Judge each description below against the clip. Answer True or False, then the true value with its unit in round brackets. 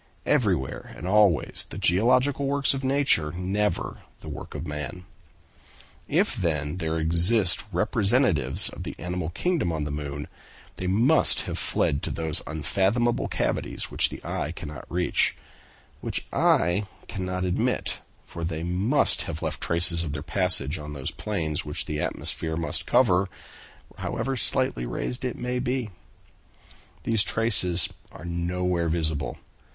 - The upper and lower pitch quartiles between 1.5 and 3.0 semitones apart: False (5.0 semitones)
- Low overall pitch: True (90 Hz)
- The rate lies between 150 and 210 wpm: False (140 wpm)